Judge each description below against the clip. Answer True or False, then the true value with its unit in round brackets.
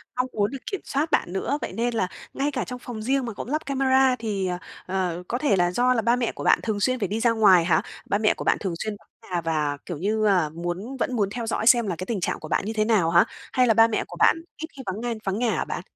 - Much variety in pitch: False (4.9 semitones)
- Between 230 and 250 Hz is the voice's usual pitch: False (220 Hz)